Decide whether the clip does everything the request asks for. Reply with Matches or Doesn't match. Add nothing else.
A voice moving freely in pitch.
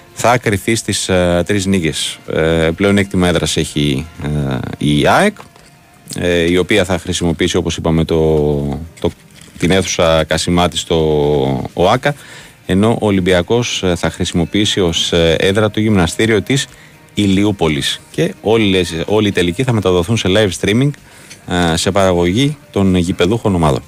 Doesn't match